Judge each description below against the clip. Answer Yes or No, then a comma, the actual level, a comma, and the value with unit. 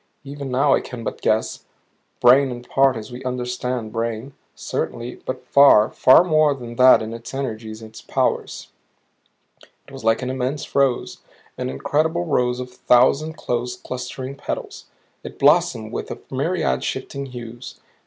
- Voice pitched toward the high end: No, low, 125 Hz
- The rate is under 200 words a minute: Yes, average, 155 wpm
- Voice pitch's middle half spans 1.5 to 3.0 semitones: Yes, average, 2.7 semitones